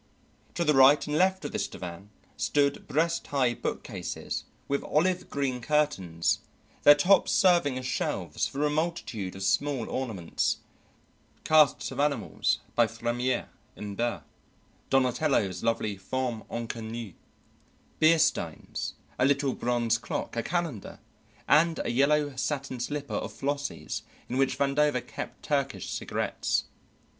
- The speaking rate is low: Yes, slow, 130 wpm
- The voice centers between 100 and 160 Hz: Yes, low, 135 Hz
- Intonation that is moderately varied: Yes, average, 4.2 semitones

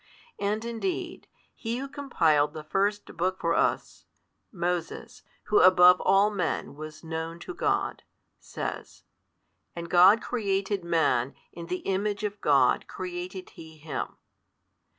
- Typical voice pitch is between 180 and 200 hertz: Yes, medium, 185 Hz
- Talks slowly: Yes, slow, 130 wpm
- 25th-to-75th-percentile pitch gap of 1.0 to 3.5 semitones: No, average, 4.0 semitones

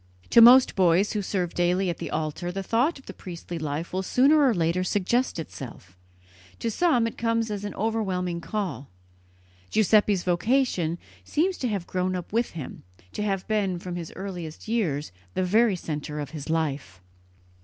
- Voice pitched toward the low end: No, medium, 185 Hz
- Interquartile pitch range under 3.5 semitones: No, average, 4.9 semitones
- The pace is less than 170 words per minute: No, average, 175 wpm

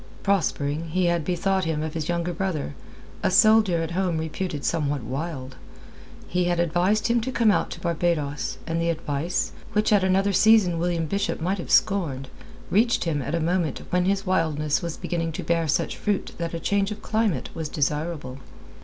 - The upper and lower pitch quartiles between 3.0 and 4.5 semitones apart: Yes, average, 3.5 semitones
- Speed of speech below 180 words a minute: No, average, 185 wpm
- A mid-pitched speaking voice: Yes, medium, 170 Hz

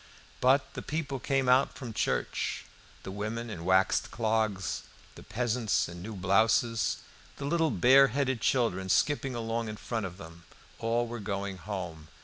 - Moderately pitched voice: No, low, 115 Hz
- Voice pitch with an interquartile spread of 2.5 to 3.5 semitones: No, average, 4.4 semitones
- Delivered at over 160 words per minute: No, average, 155 wpm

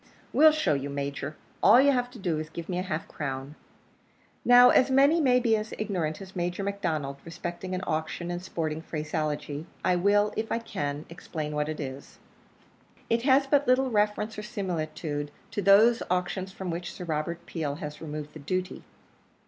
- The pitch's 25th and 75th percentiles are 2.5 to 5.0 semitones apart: No, wide, 5.6 semitones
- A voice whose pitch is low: No, medium, 175 Hz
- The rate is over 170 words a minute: Yes, average, 180 wpm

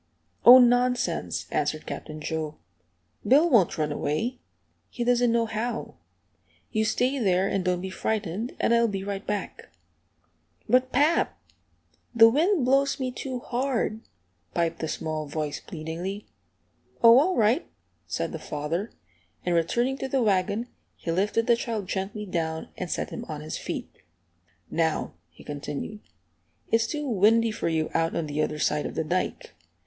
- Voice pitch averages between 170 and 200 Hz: No, high, 210 Hz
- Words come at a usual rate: Yes, average, 155 wpm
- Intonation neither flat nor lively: No, wide, 6.7 semitones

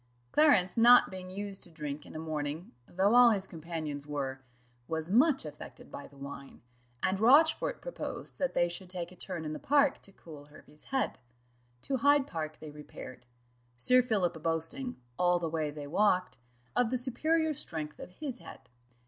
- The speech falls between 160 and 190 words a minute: Yes, average, 175 wpm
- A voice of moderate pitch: Yes, medium, 180 Hz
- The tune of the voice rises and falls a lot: Yes, wide, 8.1 semitones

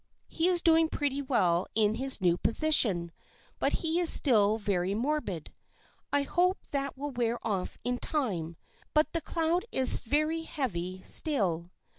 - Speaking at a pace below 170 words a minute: Yes, average, 150 wpm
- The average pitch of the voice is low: No, very high, 260 Hz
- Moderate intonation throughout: No, wide, 8.1 semitones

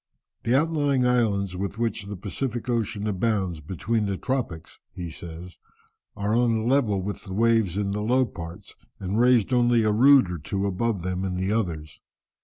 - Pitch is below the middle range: Yes, low, 105 Hz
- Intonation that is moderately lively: Yes, average, 4.1 semitones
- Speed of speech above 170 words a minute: Yes, average, 180 wpm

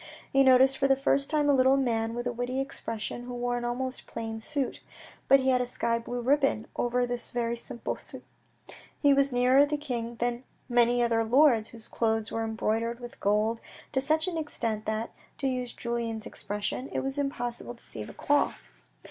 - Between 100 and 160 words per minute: No, average, 195 wpm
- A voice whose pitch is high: Yes, high, 245 Hz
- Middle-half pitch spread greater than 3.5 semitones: No, average, 2.7 semitones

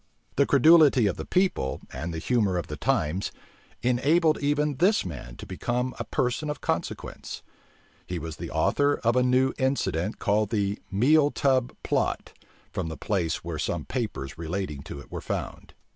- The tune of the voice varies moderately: No, wide, 8.3 semitones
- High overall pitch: No, low, 115 Hz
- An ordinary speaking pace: Yes, average, 170 wpm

